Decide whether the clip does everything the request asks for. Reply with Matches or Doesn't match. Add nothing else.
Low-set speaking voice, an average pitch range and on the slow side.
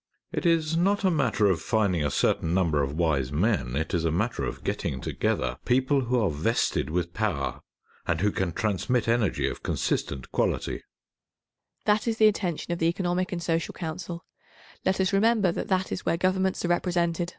Doesn't match